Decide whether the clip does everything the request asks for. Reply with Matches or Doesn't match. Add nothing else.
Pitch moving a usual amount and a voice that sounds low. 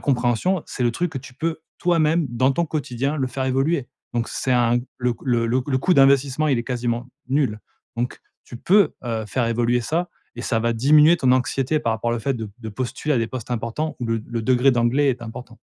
Matches